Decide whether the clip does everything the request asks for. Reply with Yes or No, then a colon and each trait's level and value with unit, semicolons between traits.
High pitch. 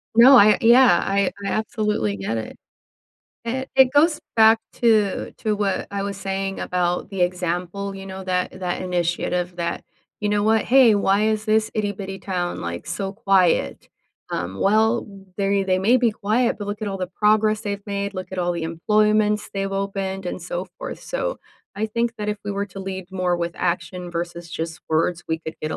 Yes: high, 195 Hz